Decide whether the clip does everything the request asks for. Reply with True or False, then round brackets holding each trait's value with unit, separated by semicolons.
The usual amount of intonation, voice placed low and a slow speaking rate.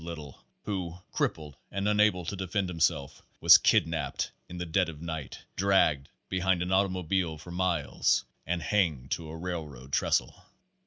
False (3.1 semitones; 85 Hz; 155 wpm)